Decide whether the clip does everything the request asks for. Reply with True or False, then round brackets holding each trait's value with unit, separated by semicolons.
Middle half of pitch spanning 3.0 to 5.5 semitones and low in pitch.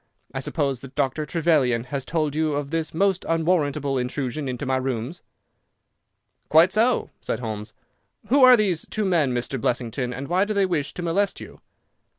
False (5.0 semitones; 150 Hz)